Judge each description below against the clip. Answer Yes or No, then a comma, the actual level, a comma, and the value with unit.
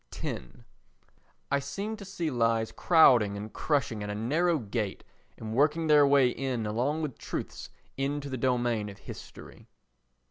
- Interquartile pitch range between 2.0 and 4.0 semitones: No, average, 4.9 semitones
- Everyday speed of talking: Yes, average, 150 wpm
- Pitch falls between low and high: No, low, 130 Hz